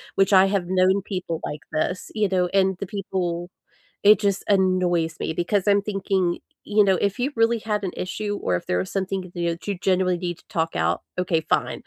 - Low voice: No, high, 190 Hz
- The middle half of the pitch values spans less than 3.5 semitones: Yes, narrow, 2.4 semitones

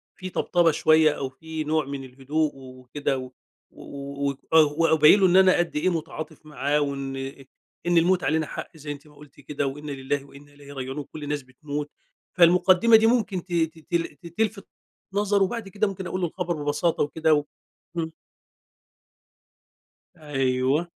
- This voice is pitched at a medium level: Yes, medium, 155 Hz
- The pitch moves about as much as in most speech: Yes, average, 3.6 semitones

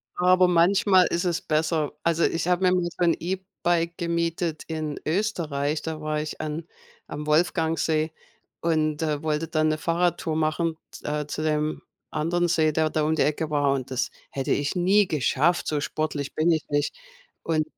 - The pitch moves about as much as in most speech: No, narrow, 2.1 semitones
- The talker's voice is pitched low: No, medium, 160 Hz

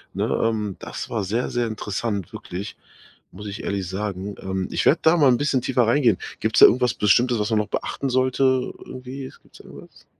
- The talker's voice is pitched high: No, low, 115 Hz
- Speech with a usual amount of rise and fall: Yes, average, 4.1 semitones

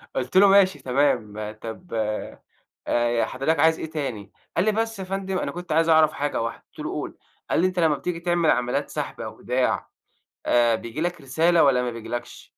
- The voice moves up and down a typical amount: No, wide, 6.7 semitones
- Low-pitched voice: No, medium, 155 Hz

